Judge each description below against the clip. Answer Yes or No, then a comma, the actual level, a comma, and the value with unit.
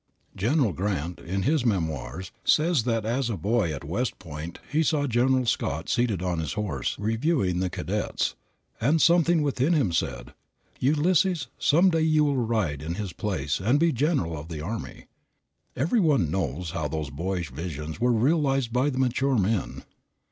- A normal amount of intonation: No, wide, 8.8 semitones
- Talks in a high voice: No, low, 110 Hz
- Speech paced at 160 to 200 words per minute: Yes, average, 170 wpm